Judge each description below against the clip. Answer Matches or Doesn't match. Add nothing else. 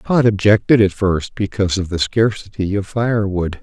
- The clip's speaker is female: Doesn't match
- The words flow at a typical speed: Matches